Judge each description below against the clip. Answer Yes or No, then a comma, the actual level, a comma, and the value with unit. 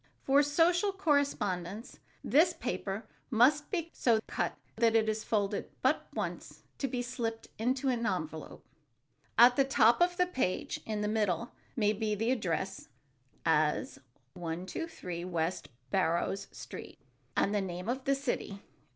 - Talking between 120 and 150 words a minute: Yes, average, 140 wpm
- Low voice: No, high, 225 Hz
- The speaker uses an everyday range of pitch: No, wide, 6.0 semitones